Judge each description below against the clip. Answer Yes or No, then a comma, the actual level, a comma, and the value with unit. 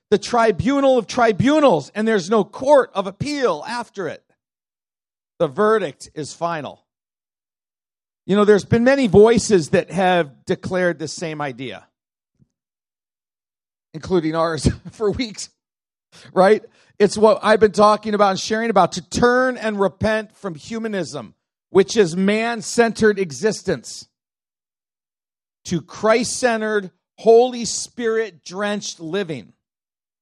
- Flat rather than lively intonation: No, average, 4.2 semitones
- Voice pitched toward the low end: No, high, 205 Hz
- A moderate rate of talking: No, slow, 115 wpm